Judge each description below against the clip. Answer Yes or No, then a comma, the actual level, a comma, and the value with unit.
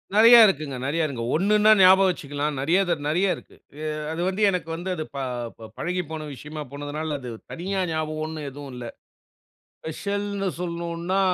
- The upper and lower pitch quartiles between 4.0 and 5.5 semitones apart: Yes, average, 4.5 semitones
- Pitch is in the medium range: Yes, medium, 160 Hz